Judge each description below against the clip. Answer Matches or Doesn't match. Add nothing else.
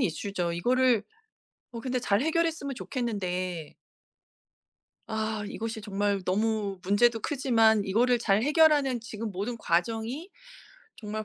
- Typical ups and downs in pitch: Matches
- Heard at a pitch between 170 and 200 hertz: Doesn't match